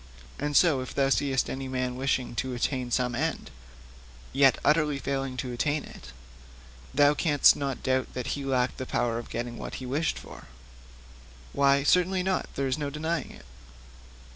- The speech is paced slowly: No, average, 170 wpm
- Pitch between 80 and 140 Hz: Yes, low, 135 Hz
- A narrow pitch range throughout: Yes, narrow, 2.3 semitones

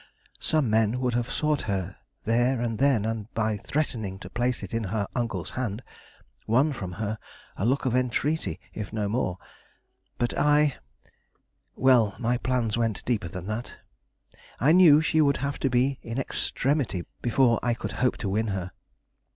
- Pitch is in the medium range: No, low, 120 Hz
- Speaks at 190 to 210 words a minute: No, average, 165 wpm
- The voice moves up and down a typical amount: Yes, average, 3.6 semitones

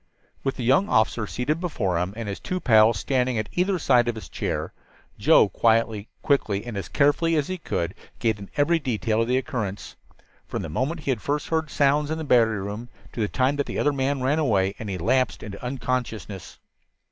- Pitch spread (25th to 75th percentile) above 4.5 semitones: Yes, average, 5.1 semitones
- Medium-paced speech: No, fast, 210 wpm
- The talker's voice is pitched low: Yes, low, 125 Hz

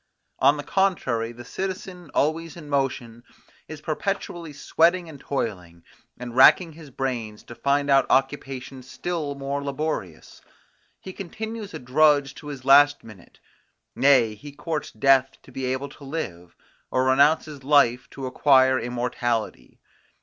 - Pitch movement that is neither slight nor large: Yes, average, 3.5 semitones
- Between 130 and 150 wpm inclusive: Yes, average, 140 wpm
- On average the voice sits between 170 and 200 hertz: No, medium, 140 Hz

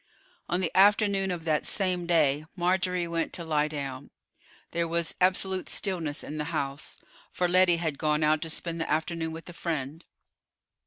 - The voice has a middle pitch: Yes, medium, 165 Hz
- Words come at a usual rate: Yes, average, 170 wpm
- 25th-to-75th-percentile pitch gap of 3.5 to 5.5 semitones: No, average, 2.8 semitones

